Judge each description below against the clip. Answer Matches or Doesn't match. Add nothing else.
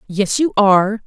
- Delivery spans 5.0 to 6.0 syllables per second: Doesn't match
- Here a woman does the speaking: Matches